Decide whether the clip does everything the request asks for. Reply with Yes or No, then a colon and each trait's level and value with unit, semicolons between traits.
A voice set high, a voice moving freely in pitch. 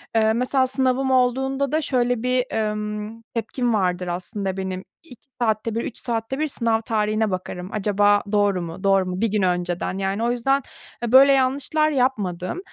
No: high, 225 Hz; average, 4.6 semitones